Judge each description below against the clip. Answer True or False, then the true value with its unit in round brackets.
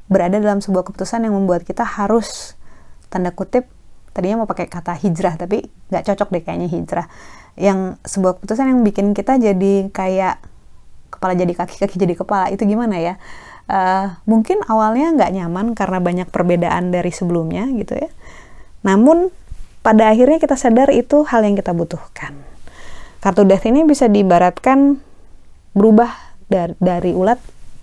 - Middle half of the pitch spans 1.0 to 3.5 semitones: False (3.9 semitones)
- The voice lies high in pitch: True (195 Hz)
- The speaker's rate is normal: False (145 wpm)